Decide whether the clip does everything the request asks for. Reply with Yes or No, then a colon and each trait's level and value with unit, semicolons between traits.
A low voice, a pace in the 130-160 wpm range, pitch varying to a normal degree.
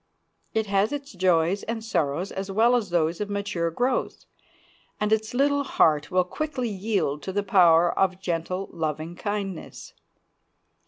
No: high, 195 Hz; average, 150 wpm; average, 4.3 semitones